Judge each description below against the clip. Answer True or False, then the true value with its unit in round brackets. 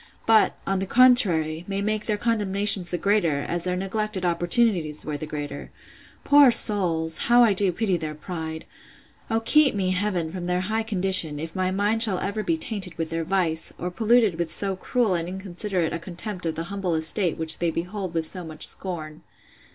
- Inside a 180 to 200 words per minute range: True (190 wpm)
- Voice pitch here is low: False (185 Hz)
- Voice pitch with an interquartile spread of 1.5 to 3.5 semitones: False (4.1 semitones)